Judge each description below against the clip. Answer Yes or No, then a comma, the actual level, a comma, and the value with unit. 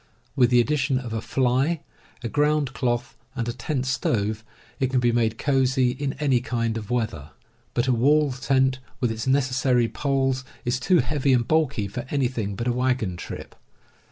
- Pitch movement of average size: No, narrow, 2.2 semitones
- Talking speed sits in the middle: Yes, average, 180 wpm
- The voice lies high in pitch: No, low, 125 Hz